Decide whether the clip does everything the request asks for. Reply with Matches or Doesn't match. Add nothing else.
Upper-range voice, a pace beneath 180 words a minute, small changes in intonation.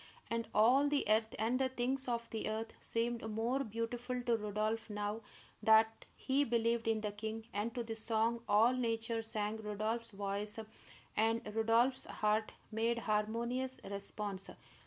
Matches